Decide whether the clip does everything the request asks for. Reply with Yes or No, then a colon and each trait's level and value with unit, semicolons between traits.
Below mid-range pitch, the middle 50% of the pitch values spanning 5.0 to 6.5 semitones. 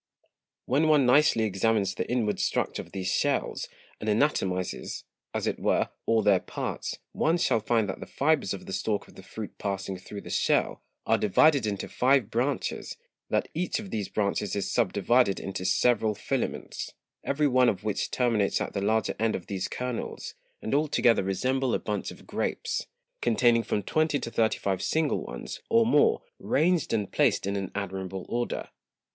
Yes: low, 110 Hz; wide, 5.5 semitones